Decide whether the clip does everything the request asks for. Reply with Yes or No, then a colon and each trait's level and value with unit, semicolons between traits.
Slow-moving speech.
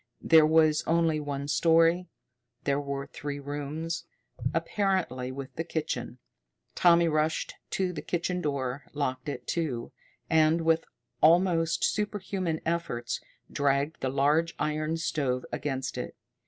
Yes: slow, 130 wpm